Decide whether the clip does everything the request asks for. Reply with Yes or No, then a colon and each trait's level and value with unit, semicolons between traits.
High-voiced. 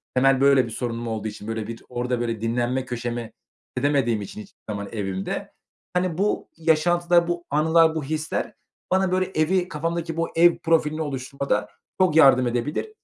No: medium, 140 Hz